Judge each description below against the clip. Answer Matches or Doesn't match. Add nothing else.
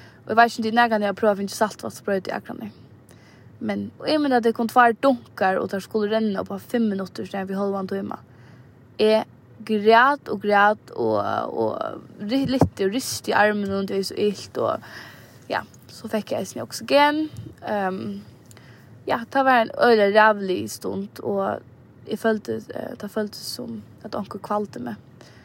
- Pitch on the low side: Doesn't match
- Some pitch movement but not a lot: Matches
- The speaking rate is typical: Matches